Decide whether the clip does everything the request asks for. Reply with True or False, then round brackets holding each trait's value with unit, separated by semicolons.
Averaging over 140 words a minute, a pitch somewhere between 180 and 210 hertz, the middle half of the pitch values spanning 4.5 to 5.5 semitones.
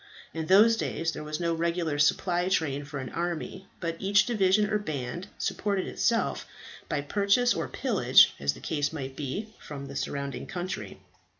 False (170 wpm; 170 Hz; 5.1 semitones)